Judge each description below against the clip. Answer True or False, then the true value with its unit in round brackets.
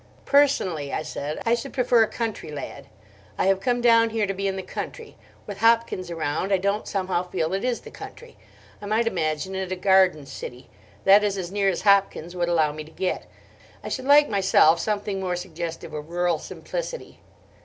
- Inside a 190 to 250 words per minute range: True (195 wpm)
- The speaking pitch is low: False (190 Hz)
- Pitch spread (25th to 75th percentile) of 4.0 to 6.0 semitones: True (4.6 semitones)